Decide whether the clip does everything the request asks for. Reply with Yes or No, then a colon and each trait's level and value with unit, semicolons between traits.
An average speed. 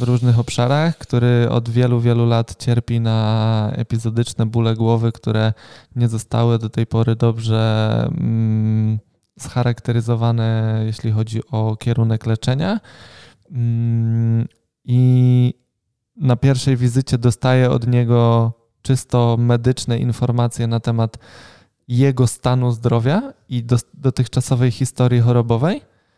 No: slow, 105 wpm